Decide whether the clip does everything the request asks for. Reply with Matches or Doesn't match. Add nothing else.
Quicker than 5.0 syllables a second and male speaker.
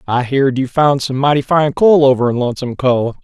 Matches